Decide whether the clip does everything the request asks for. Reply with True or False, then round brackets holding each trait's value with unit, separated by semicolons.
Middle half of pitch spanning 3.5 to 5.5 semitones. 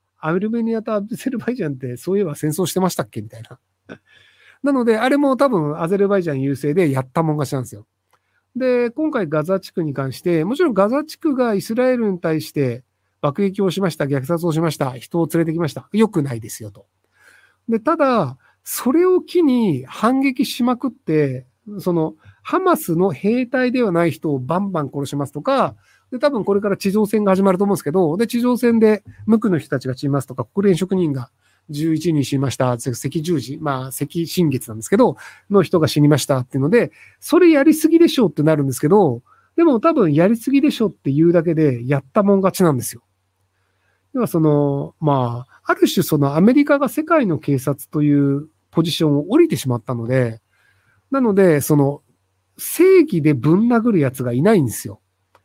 False (8.3 semitones)